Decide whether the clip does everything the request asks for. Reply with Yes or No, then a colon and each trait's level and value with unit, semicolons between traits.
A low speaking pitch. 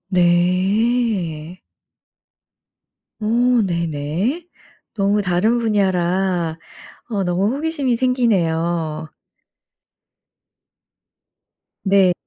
No: high, 190 Hz